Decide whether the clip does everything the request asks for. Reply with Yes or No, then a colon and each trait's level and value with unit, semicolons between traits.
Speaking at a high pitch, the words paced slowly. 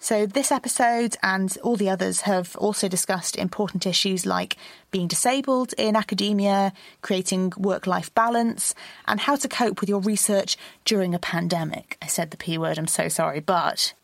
No: high, 200 Hz; average, 170 wpm